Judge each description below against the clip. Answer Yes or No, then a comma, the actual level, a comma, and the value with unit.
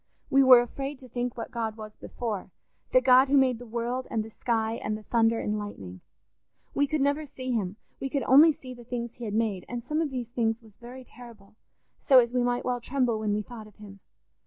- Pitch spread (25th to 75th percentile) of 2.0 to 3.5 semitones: Yes, average, 2.8 semitones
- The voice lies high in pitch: Yes, high, 240 Hz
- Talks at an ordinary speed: No, fast, 230 wpm